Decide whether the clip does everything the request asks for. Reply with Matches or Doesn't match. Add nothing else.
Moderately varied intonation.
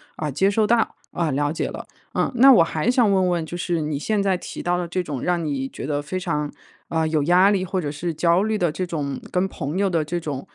Matches